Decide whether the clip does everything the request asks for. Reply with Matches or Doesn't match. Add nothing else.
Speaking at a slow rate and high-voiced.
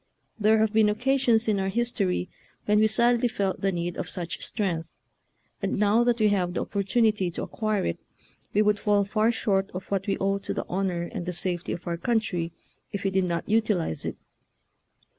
Doesn't match